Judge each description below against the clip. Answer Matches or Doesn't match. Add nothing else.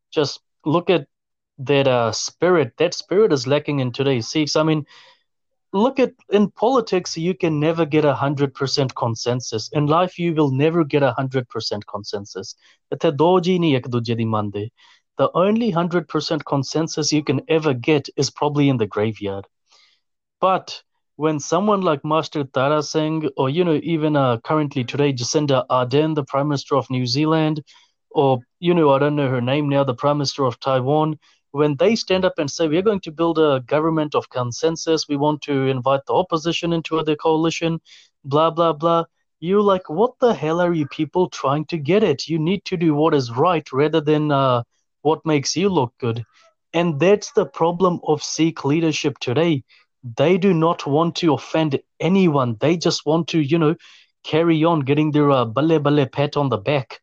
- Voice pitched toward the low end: Doesn't match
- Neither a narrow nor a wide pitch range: Matches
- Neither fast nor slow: Matches